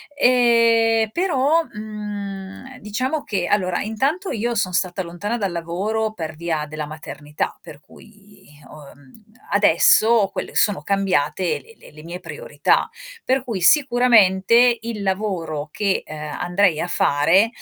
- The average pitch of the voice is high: Yes, high, 200 Hz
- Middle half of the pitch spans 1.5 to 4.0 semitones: No, average, 5.2 semitones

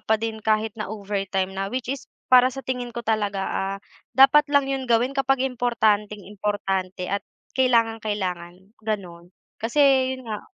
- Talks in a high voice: Yes, high, 220 Hz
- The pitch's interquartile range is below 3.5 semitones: No, average, 4.2 semitones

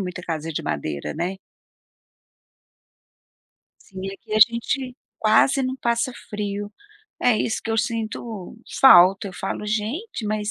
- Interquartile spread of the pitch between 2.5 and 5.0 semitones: Yes, average, 3.6 semitones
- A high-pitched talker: Yes, high, 215 Hz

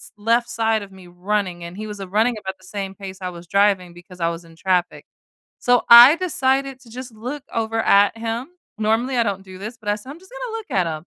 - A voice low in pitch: No, high, 210 Hz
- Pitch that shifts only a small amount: No, average, 4.4 semitones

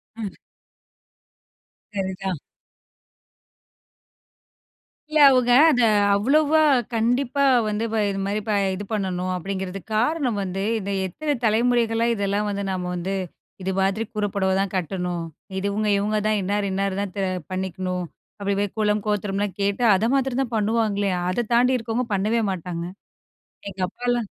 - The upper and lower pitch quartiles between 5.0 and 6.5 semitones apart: No, average, 3.3 semitones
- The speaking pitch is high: Yes, high, 205 Hz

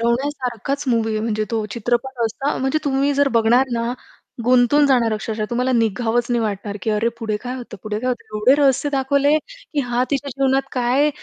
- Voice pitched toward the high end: Yes, high, 245 Hz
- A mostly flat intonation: No, average, 3.2 semitones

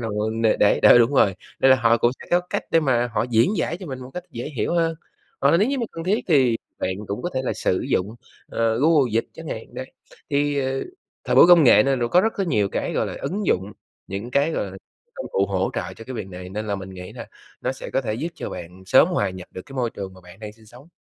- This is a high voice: No, low, 120 Hz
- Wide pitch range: Yes, wide, 6.6 semitones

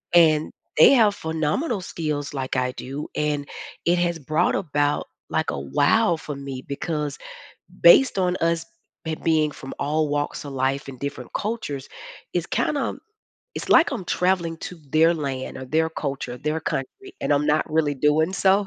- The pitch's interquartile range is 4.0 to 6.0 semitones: No, average, 3.4 semitones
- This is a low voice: No, medium, 155 Hz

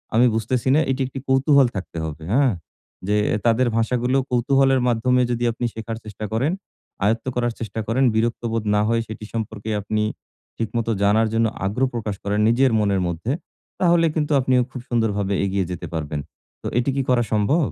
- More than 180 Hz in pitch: No, low, 115 Hz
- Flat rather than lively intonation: No, average, 3.2 semitones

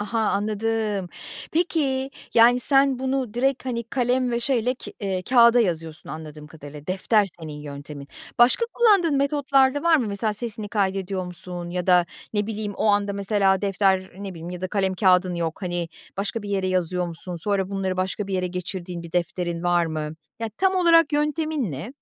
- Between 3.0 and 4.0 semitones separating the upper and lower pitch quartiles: No, wide, 5.4 semitones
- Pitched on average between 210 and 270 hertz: No, high, 200 Hz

